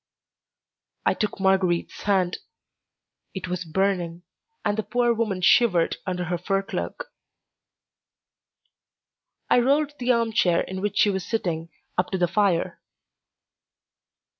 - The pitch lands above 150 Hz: Yes, high, 190 Hz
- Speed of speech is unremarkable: No, slow, 125 wpm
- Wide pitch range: No, average, 3.7 semitones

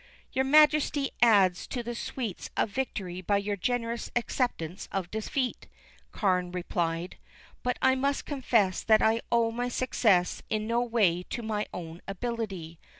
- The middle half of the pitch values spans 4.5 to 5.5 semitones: Yes, average, 4.9 semitones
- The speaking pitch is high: Yes, high, 220 Hz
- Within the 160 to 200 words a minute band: No, average, 150 wpm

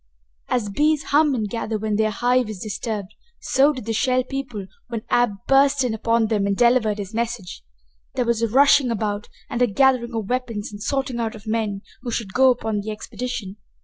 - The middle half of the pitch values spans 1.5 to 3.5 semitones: Yes, average, 3.0 semitones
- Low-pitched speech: No, high, 230 Hz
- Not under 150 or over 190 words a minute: No, average, 200 wpm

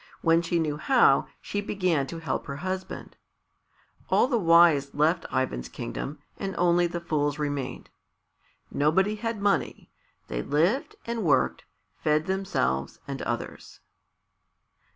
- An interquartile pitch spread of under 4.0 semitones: No, average, 4.7 semitones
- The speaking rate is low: Yes, slow, 130 wpm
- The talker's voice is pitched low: No, medium, 165 Hz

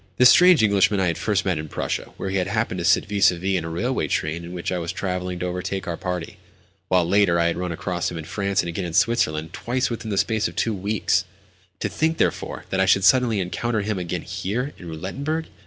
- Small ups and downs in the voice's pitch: No, average, 3.6 semitones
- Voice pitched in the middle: No, very low, 95 Hz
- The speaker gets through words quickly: Yes, fast, 240 wpm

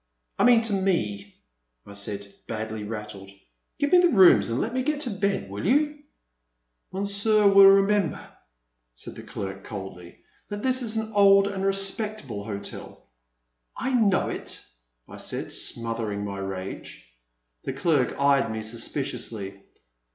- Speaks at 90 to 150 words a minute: Yes, average, 145 wpm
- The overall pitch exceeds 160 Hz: No, medium, 140 Hz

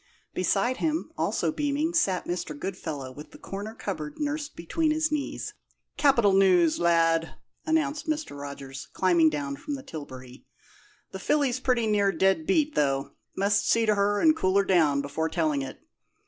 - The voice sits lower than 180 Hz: No, high, 195 Hz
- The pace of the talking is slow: No, average, 160 wpm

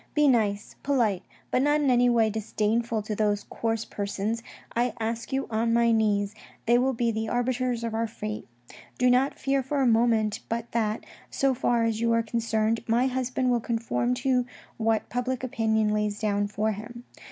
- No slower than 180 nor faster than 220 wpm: Yes, average, 185 wpm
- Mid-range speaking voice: No, high, 230 Hz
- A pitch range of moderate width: No, narrow, 2.2 semitones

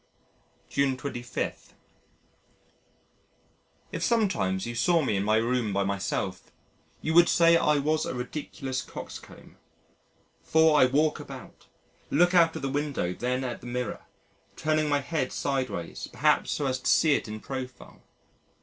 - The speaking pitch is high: No, low, 135 Hz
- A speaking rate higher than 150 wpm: No, average, 145 wpm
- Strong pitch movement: No, average, 4.3 semitones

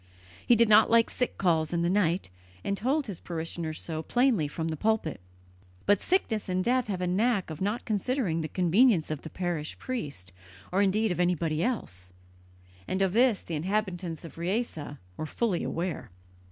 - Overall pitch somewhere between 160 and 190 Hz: Yes, medium, 185 Hz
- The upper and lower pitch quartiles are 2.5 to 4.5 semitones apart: No, average, 5.3 semitones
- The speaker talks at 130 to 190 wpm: Yes, average, 180 wpm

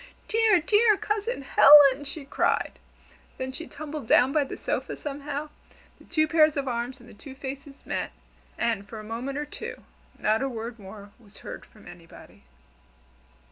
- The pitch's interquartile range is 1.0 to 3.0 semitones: No, average, 4.6 semitones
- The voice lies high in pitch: Yes, very high, 275 Hz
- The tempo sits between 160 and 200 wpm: Yes, average, 170 wpm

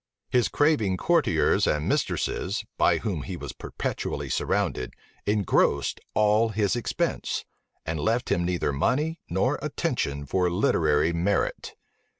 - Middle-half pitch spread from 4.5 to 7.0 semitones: Yes, average, 5.2 semitones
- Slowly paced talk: Yes, slow, 125 wpm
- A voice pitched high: No, very low, 95 Hz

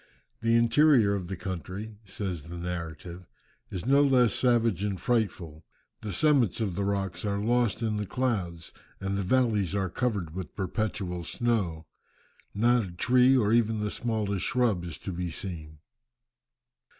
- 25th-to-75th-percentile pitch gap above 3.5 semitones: Yes, average, 4.7 semitones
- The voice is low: Yes, low, 100 Hz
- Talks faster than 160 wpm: No, average, 155 wpm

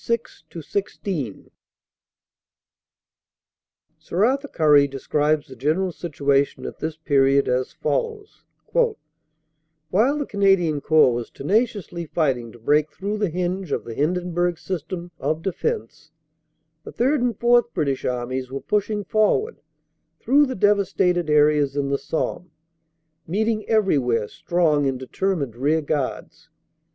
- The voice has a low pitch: No, medium, 160 Hz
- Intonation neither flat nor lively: No, wide, 6.0 semitones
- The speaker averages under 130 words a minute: Yes, slow, 120 wpm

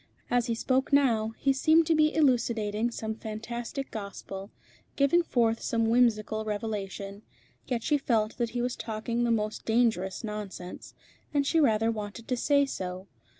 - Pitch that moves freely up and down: No, average, 2.9 semitones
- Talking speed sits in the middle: Yes, average, 155 wpm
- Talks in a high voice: Yes, high, 230 Hz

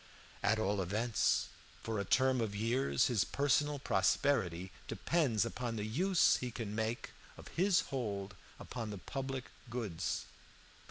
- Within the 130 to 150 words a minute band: Yes, average, 140 wpm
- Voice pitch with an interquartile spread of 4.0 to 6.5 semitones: Yes, average, 4.4 semitones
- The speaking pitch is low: Yes, low, 115 Hz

